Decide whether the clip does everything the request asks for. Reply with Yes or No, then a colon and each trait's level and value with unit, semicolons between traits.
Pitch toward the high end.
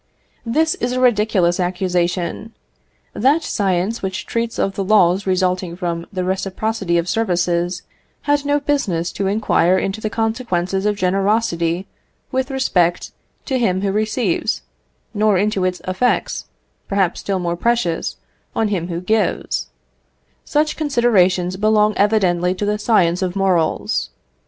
Yes: high, 195 Hz